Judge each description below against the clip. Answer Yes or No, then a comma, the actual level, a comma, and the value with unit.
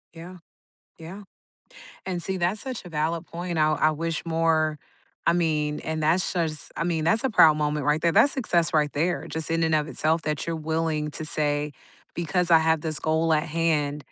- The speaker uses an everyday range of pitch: No, narrow, 1.8 semitones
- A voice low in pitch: No, medium, 160 Hz